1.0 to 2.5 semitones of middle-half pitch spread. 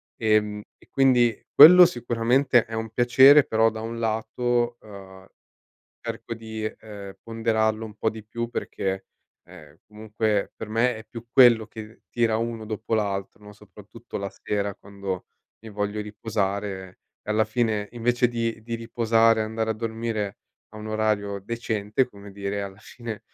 Yes: narrow, 2.0 semitones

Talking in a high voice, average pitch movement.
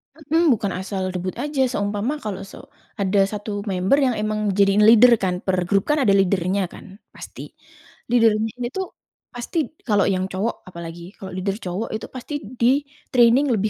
Yes: high, 205 Hz; average, 3.7 semitones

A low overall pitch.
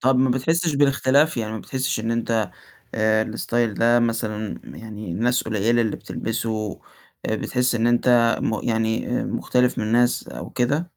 Yes: low, 115 Hz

